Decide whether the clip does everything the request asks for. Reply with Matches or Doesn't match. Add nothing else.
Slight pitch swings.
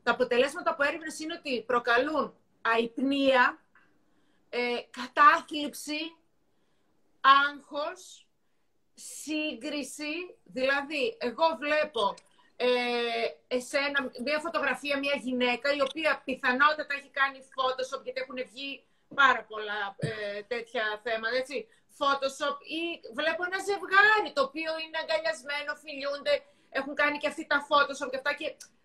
Doesn't match